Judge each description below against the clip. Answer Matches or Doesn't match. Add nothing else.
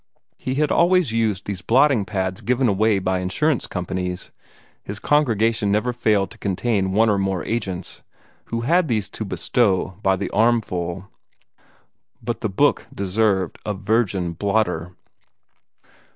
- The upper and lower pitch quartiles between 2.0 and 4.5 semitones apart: Matches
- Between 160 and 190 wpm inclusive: Doesn't match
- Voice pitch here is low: Matches